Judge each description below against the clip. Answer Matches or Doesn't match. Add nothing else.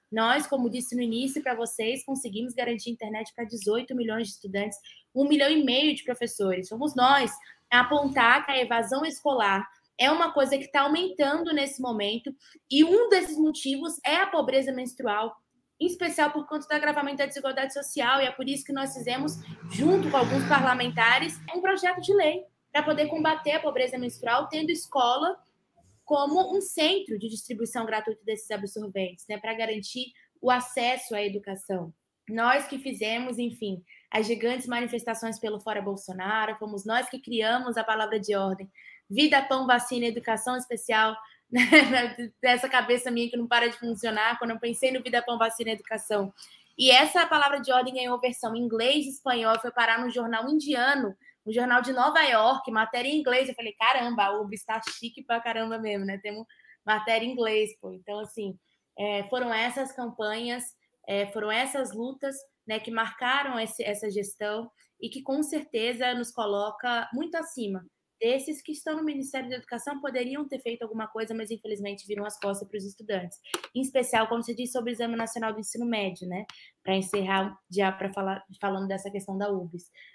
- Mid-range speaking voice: Doesn't match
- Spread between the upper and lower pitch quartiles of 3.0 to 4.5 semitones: Matches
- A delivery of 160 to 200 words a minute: Matches